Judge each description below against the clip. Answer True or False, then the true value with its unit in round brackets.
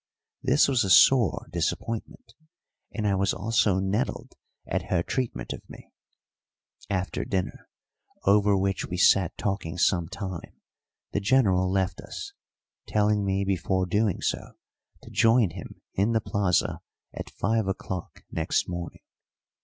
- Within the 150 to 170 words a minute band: False (135 wpm)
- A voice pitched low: True (100 Hz)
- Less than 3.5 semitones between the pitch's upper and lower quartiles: True (2.6 semitones)